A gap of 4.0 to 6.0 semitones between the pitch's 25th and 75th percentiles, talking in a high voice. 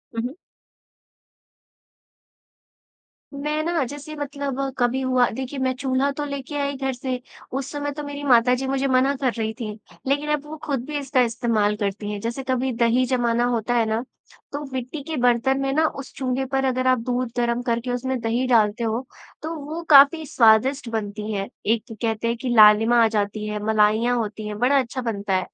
No: average, 3.2 semitones; very high, 250 Hz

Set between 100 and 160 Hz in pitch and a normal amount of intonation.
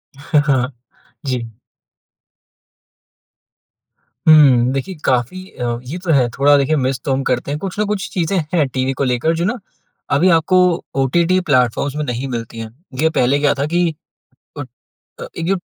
Yes: medium, 140 Hz; average, 4.4 semitones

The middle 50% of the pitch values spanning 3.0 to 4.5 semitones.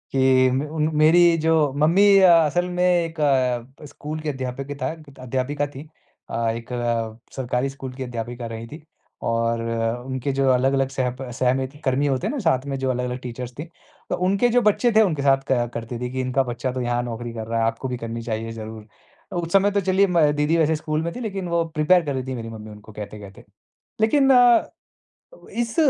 No: average, 4.9 semitones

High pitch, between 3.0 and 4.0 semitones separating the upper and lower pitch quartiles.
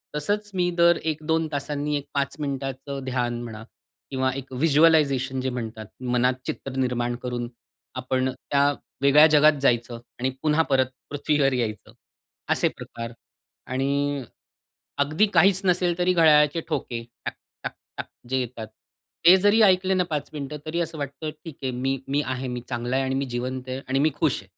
No: medium, 140 Hz; average, 3.4 semitones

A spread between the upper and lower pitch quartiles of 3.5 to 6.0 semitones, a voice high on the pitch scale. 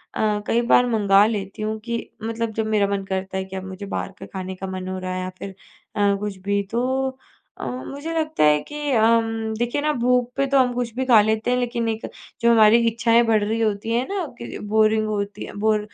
No: average, 2.9 semitones; high, 220 Hz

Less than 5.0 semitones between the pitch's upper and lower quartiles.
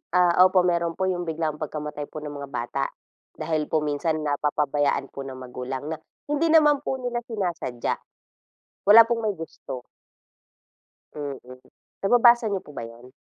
No: wide, 5.4 semitones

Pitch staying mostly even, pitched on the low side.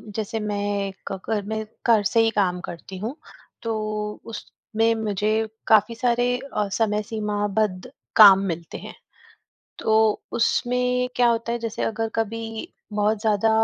No: narrow, 1.8 semitones; high, 220 Hz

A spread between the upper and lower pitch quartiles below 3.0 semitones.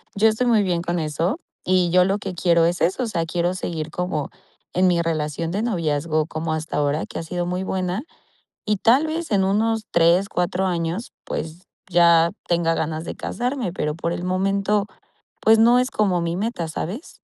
No: average, 3.4 semitones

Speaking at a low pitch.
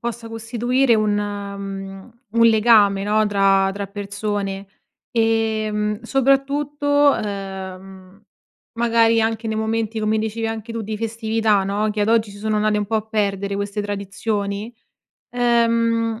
No: high, 215 Hz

